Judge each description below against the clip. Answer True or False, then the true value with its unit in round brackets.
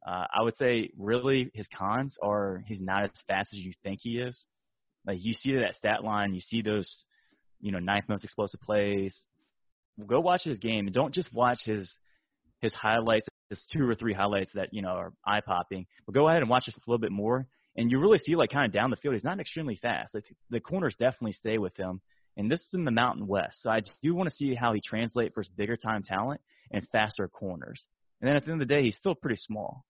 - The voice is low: True (110 Hz)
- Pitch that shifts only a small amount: False (4.0 semitones)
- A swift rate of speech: True (245 wpm)